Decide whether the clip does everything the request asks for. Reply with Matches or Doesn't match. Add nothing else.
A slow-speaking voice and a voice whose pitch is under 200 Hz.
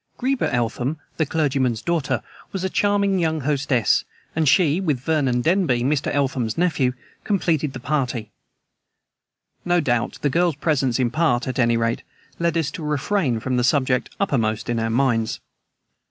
Doesn't match